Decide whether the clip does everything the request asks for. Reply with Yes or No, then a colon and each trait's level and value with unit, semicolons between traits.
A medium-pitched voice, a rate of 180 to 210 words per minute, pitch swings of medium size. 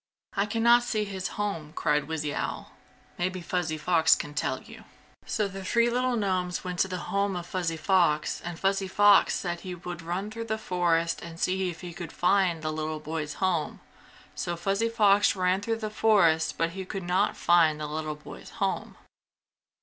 Yes: medium, 180 Hz; average, 190 wpm; average, 3.4 semitones